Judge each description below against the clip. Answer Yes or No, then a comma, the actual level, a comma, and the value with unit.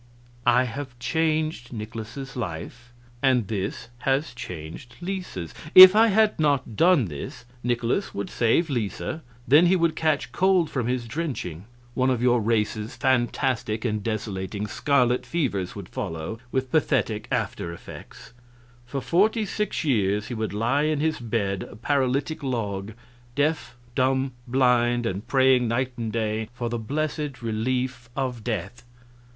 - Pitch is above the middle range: No, low, 125 Hz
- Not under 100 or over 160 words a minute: Yes, average, 145 wpm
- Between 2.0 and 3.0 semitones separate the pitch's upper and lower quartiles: No, average, 4.4 semitones